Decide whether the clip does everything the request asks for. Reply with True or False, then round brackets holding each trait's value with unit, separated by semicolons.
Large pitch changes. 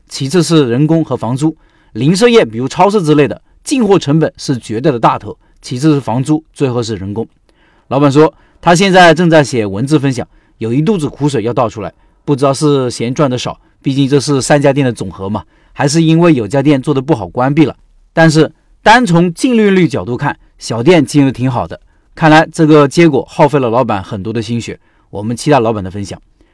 False (4.9 semitones)